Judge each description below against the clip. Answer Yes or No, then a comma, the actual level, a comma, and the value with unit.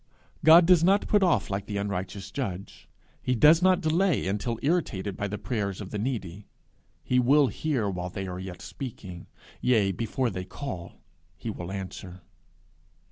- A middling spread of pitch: No, wide, 6.9 semitones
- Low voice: Yes, low, 105 Hz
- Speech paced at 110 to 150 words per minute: No, average, 165 wpm